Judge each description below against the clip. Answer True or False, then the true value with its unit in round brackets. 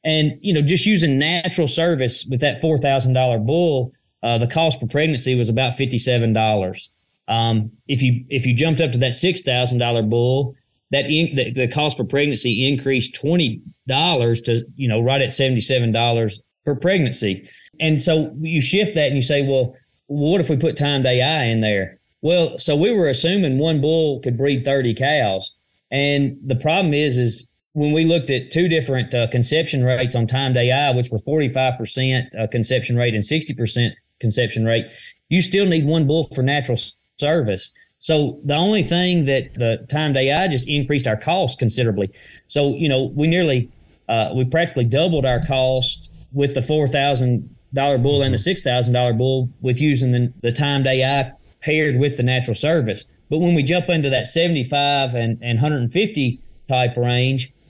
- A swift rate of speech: False (180 wpm)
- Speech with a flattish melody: False (3.7 semitones)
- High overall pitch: False (135 Hz)